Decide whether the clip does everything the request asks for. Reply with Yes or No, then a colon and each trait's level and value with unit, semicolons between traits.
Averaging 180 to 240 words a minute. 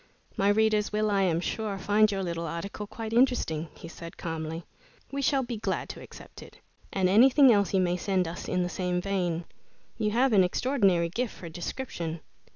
Yes: average, 190 wpm